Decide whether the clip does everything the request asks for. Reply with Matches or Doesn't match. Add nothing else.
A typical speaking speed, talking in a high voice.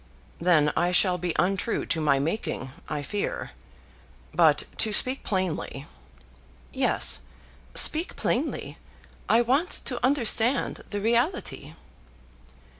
Doesn't match